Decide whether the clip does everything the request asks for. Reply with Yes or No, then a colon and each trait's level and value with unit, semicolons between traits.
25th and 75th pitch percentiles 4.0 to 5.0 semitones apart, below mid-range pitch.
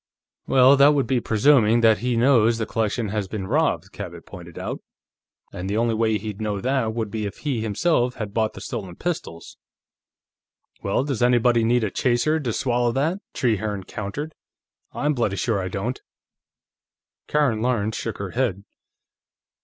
No: average, 3.3 semitones; low, 115 Hz